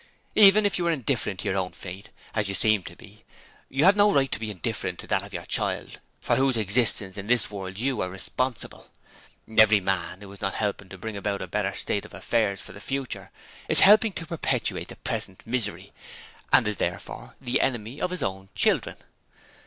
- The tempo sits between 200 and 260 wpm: Yes, fast, 205 wpm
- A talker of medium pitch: No, low, 110 Hz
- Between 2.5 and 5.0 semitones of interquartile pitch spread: No, wide, 5.5 semitones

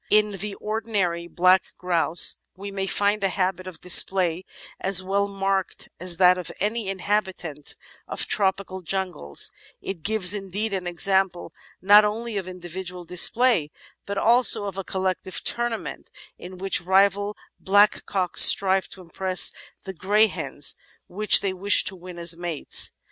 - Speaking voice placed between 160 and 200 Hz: Yes, high, 190 Hz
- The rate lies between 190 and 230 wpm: No, average, 145 wpm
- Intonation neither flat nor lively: No, narrow, 1.9 semitones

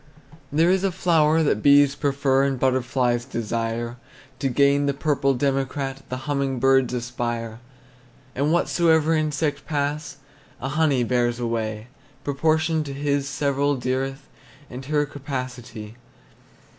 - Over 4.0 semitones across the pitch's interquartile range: No, average, 2.9 semitones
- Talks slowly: Yes, slow, 125 wpm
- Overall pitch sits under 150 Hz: Yes, low, 135 Hz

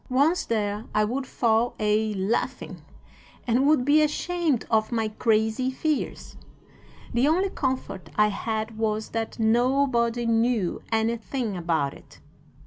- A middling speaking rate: No, slow, 130 wpm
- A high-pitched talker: Yes, high, 230 Hz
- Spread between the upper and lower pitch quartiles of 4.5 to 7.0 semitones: No, average, 3.3 semitones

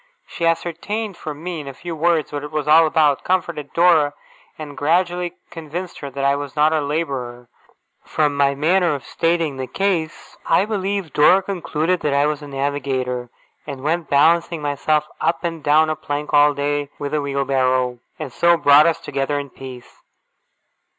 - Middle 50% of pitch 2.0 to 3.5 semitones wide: Yes, average, 3.0 semitones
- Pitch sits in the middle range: Yes, medium, 150 Hz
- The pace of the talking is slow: No, average, 175 wpm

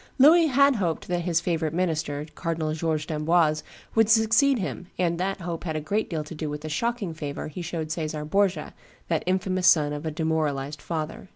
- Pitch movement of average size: Yes, average, 3.3 semitones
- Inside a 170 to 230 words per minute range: Yes, average, 195 wpm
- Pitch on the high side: No, medium, 165 Hz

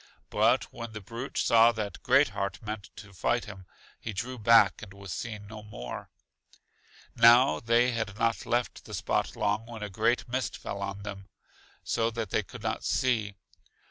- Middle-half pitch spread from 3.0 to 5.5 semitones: No, narrow, 2.4 semitones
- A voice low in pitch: Yes, low, 110 Hz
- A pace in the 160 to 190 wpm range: Yes, average, 175 wpm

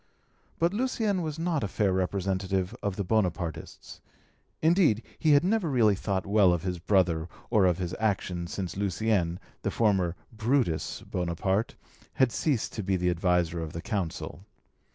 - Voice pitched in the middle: No, very low, 95 Hz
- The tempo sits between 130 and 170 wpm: Yes, average, 155 wpm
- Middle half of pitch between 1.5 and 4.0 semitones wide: No, average, 4.5 semitones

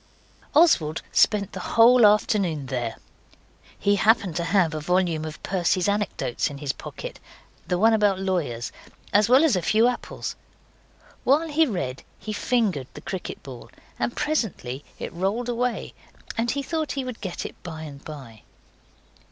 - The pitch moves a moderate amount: No, wide, 7.0 semitones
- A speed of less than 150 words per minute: No, average, 160 wpm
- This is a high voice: Yes, high, 195 Hz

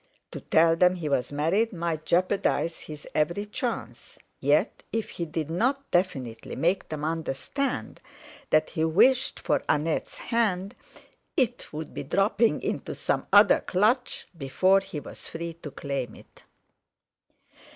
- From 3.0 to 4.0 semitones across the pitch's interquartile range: No, average, 4.8 semitones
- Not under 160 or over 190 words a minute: No, average, 140 wpm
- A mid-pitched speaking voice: Yes, medium, 170 Hz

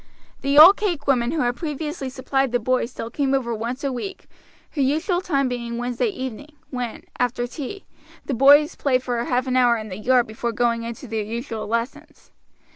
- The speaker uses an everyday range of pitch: Yes, average, 3.1 semitones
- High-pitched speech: Yes, very high, 255 Hz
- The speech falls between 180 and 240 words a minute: Yes, average, 195 wpm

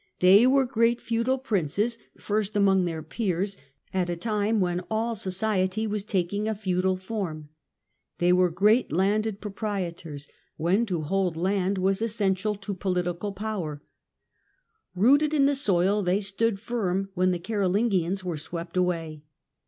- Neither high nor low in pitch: No, high, 195 Hz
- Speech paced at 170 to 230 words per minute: No, average, 155 wpm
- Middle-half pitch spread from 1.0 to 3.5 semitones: Yes, average, 3.2 semitones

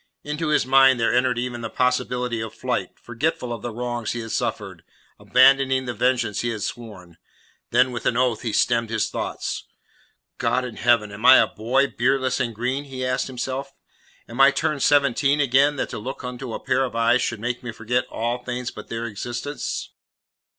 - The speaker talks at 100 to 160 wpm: No, average, 190 wpm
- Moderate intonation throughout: No, narrow, 2.1 semitones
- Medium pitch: No, low, 125 Hz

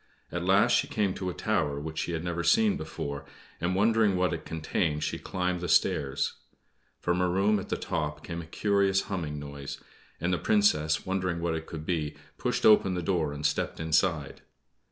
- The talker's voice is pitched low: Yes, very low, 85 Hz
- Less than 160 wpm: No, average, 195 wpm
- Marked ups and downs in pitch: No, average, 3.6 semitones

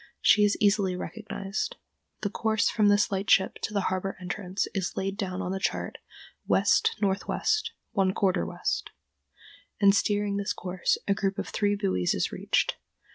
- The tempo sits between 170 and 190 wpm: No, average, 160 wpm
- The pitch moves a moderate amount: No, narrow, 1.5 semitones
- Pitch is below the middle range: No, high, 200 Hz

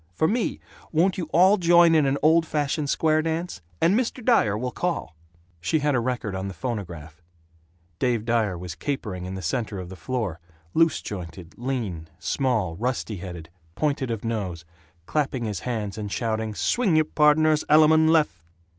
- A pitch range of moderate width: No, wide, 8.3 semitones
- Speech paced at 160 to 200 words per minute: Yes, average, 170 wpm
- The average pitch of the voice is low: Yes, low, 125 Hz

